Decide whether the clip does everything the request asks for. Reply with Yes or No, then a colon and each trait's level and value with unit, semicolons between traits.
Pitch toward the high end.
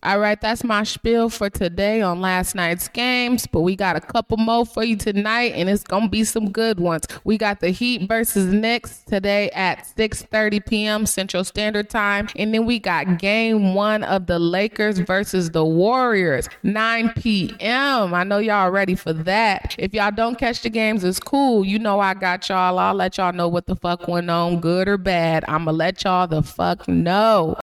Yes: high, 200 Hz